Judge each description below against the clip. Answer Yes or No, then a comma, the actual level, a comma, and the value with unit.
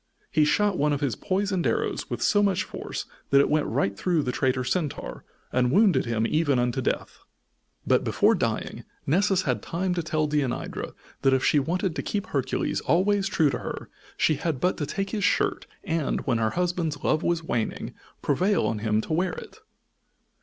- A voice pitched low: No, medium, 155 Hz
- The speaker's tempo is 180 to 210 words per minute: Yes, average, 190 wpm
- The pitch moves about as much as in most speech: No, wide, 5.7 semitones